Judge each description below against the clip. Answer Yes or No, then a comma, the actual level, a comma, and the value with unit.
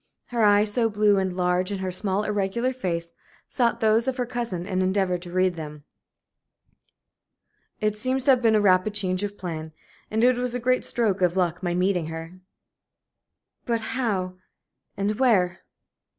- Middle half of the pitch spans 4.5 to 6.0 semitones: No, average, 3.9 semitones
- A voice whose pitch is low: No, high, 200 Hz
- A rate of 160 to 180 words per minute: Yes, average, 170 wpm